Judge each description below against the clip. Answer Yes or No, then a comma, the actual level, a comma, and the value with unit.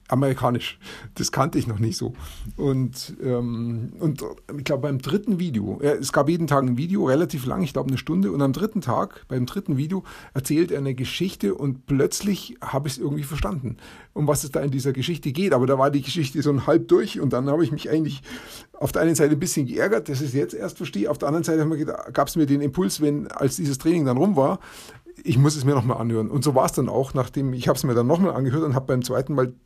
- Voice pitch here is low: No, medium, 145 Hz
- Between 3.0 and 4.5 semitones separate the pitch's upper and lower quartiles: Yes, average, 3.3 semitones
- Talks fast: Yes, fast, 250 wpm